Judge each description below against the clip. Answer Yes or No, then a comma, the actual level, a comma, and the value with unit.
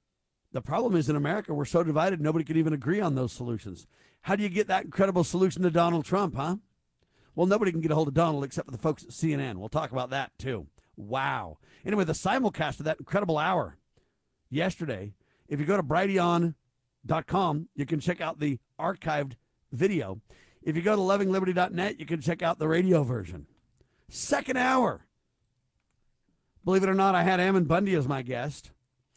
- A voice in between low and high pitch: Yes, medium, 160 Hz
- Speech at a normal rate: Yes, average, 185 wpm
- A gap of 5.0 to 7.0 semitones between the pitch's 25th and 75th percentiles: Yes, average, 5.3 semitones